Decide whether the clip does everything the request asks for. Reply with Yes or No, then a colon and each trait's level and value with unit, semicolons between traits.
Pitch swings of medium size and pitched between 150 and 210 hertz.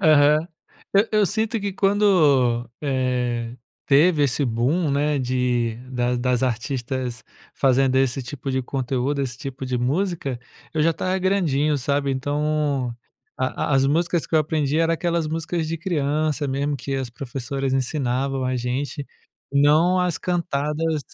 No: average, 3.5 semitones; medium, 140 Hz